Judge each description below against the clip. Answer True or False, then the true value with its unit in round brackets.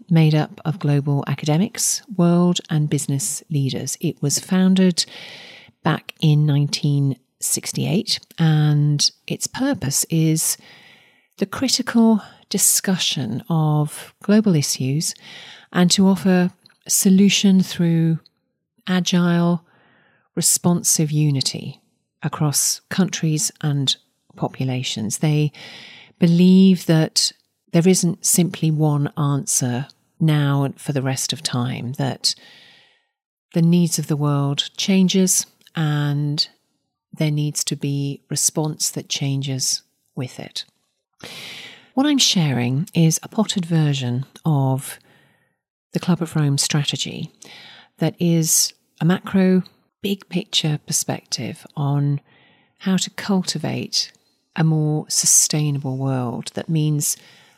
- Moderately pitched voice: True (160 Hz)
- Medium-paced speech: False (100 wpm)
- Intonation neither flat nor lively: True (4.0 semitones)